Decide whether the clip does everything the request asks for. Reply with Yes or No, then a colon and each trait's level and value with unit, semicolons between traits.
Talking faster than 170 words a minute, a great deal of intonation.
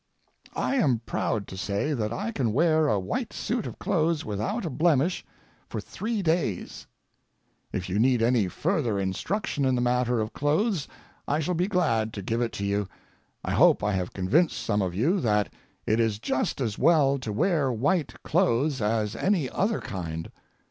Yes: average, 180 wpm; wide, 7.9 semitones